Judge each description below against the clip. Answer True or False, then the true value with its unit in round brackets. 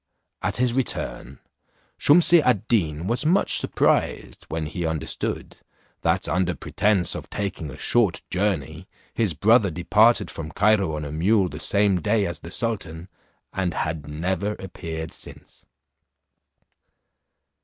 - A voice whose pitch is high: False (95 Hz)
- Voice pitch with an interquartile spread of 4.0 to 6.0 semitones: True (5.0 semitones)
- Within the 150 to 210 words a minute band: False (135 wpm)